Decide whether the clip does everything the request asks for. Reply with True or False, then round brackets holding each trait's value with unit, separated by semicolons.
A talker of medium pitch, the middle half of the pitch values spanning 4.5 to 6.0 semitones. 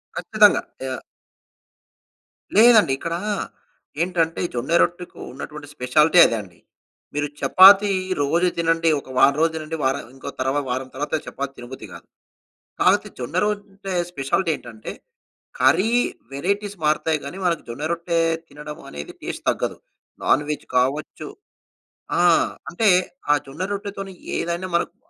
True (160 Hz; 5.1 semitones)